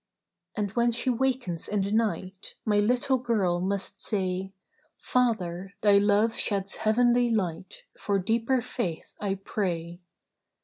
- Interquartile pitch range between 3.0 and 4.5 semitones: Yes, average, 3.8 semitones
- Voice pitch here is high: Yes, high, 205 Hz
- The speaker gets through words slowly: Yes, slow, 130 wpm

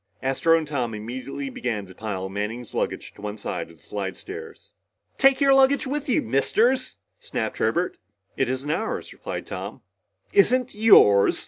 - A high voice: No, low, 135 Hz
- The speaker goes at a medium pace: Yes, average, 155 wpm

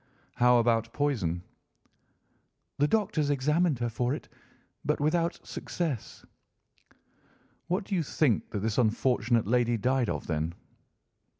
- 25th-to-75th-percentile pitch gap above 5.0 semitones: No, average, 4.7 semitones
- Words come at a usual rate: No, slow, 120 wpm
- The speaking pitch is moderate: No, low, 125 Hz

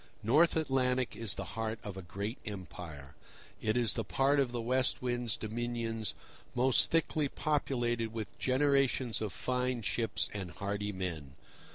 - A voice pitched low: Yes, low, 120 Hz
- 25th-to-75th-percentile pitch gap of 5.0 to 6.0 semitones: No, average, 3.8 semitones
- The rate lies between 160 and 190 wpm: No, average, 150 wpm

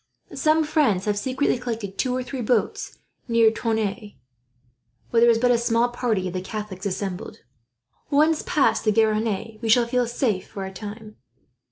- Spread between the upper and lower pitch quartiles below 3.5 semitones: Yes, average, 2.9 semitones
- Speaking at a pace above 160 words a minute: Yes, average, 170 wpm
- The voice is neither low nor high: No, high, 225 Hz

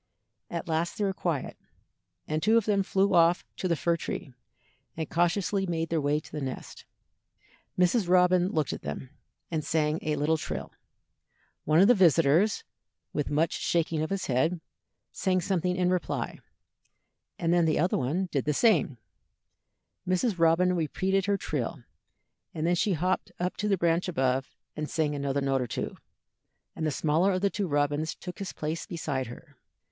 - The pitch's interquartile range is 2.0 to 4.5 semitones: Yes, average, 3.4 semitones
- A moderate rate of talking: Yes, average, 175 wpm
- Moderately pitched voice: Yes, medium, 165 Hz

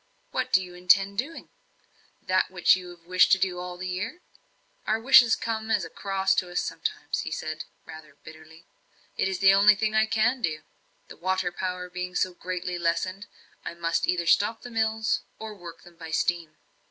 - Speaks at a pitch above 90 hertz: Yes, medium, 185 Hz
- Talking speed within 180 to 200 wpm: Yes, average, 190 wpm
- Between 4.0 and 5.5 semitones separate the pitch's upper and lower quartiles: No, average, 3.2 semitones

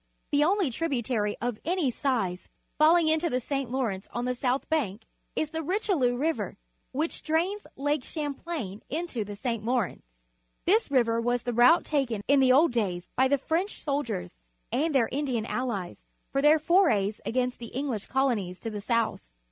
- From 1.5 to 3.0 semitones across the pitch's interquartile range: No, average, 5.0 semitones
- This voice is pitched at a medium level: No, very high, 260 Hz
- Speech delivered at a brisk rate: No, average, 170 wpm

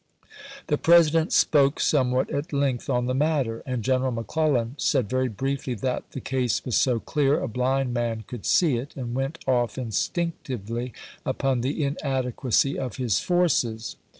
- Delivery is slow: No, average, 160 wpm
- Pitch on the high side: No, low, 130 Hz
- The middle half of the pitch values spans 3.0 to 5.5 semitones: No, narrow, 2.6 semitones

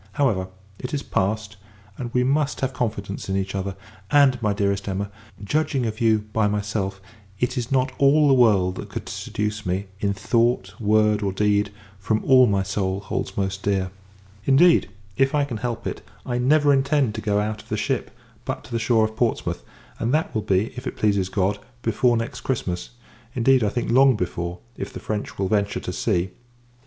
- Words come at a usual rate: Yes, average, 195 wpm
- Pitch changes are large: No, average, 4.2 semitones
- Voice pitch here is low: Yes, low, 110 Hz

